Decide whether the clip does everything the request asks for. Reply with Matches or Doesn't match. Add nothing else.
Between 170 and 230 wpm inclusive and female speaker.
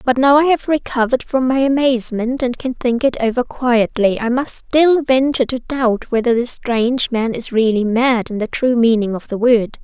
Matches